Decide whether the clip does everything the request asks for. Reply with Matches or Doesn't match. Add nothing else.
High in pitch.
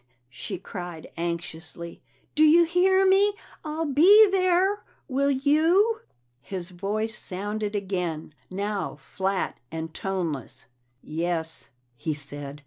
Matches